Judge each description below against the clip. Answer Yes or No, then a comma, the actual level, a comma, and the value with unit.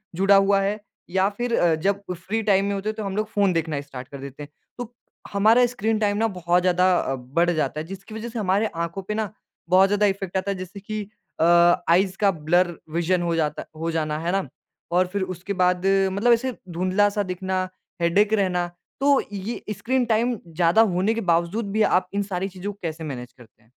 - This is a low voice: No, high, 190 Hz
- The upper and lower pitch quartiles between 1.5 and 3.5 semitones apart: Yes, average, 3.1 semitones